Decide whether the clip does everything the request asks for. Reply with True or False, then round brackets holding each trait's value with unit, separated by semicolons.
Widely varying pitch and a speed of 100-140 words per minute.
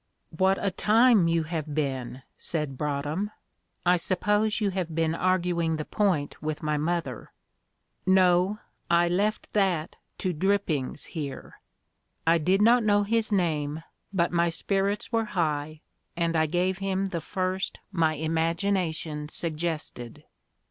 False (3.7 semitones; 135 wpm)